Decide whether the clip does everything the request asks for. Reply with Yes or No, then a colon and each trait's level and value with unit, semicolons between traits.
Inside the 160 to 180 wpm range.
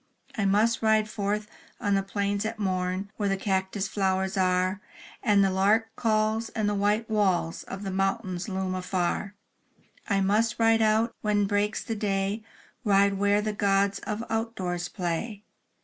Yes: average, 165 wpm